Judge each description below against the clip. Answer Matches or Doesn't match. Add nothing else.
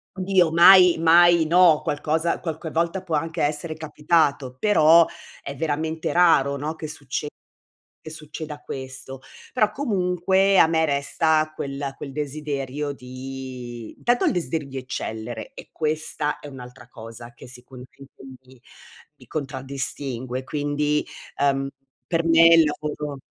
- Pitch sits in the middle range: Matches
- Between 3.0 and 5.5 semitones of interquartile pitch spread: Matches